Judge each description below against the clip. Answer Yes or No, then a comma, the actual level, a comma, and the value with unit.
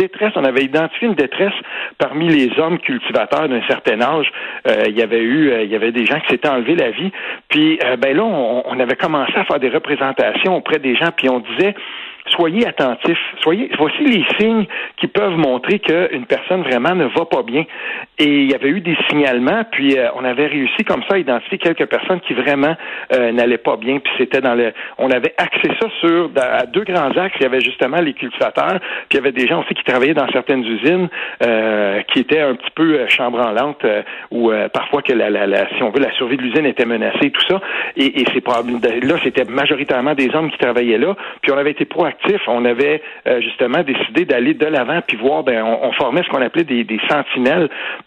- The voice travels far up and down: Yes, wide, 6.8 semitones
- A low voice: No, medium, 145 Hz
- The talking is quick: Yes, fast, 225 wpm